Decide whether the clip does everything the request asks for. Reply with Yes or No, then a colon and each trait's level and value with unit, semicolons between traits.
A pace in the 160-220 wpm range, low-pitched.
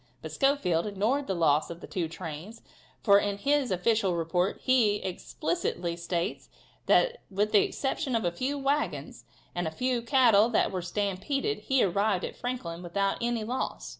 No: average, 170 wpm; high, 205 Hz